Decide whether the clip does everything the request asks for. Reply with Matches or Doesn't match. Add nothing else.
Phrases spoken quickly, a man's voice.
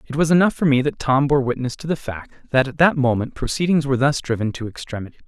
Matches